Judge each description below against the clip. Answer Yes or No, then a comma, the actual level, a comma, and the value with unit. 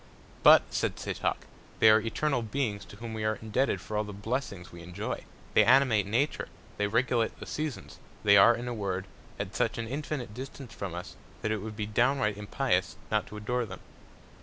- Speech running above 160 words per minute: Yes, average, 195 wpm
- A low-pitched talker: Yes, low, 110 Hz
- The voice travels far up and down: No, average, 3.2 semitones